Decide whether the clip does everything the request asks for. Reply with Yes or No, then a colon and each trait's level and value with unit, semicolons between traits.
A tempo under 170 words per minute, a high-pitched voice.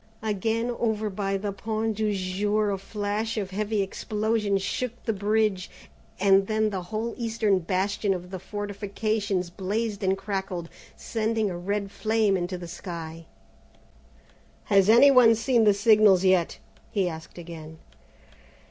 Yes: average, 140 wpm; high, 205 Hz